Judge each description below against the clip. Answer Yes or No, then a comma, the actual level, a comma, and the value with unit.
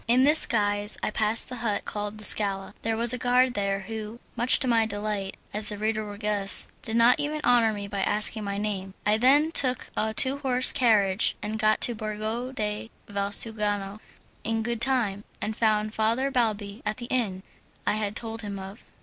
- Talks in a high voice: Yes, high, 215 Hz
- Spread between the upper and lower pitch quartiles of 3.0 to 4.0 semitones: No, narrow, 2.6 semitones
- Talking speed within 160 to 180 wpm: No, average, 195 wpm